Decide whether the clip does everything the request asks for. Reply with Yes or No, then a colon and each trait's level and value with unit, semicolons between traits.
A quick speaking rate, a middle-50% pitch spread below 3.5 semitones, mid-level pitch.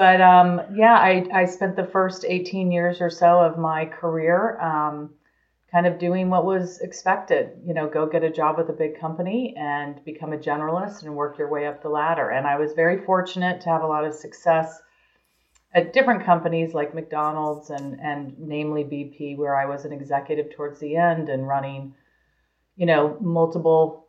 No: average, 190 wpm; average, 3.0 semitones; medium, 160 Hz